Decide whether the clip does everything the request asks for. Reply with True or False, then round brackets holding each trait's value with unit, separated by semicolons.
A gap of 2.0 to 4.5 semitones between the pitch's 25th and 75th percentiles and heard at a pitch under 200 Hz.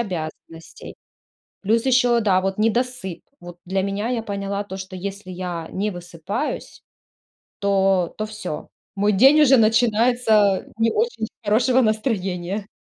False (3.3 semitones; 205 Hz)